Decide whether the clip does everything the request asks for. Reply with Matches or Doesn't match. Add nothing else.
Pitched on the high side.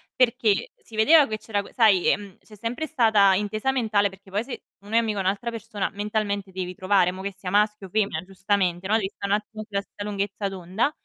Matches